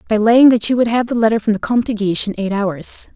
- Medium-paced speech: No, fast, 305 wpm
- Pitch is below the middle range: No, high, 220 Hz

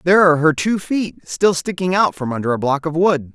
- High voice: No, medium, 165 Hz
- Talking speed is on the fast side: Yes, fast, 250 wpm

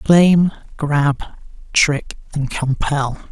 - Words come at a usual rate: No, slow, 90 wpm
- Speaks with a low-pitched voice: No, medium, 150 Hz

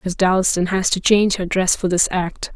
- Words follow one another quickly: Yes, fast, 235 wpm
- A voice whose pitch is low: No, medium, 185 Hz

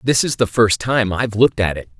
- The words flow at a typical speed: No, fast, 270 wpm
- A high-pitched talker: No, low, 110 Hz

